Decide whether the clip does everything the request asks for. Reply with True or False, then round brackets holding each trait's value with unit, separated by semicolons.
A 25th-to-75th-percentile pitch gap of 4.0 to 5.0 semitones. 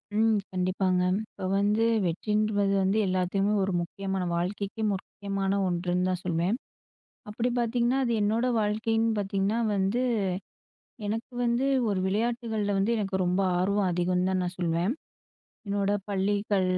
False (2.8 semitones)